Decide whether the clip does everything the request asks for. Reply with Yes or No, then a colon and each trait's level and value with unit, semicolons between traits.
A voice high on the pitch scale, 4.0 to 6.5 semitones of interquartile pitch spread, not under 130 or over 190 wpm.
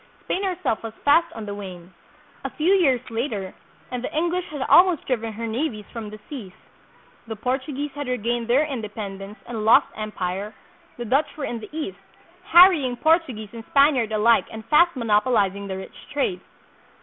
Yes: high, 235 Hz; wide, 5.5 semitones; average, 175 wpm